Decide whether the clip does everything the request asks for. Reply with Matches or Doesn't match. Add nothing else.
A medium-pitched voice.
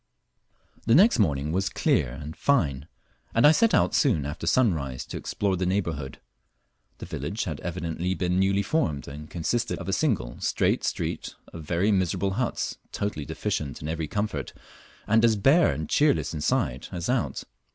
Doesn't match